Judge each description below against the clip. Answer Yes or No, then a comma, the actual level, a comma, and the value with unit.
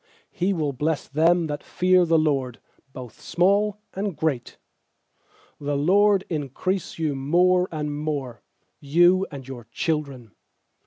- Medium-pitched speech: Yes, medium, 155 Hz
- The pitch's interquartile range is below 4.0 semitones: No, average, 4.6 semitones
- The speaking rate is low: Yes, slow, 125 wpm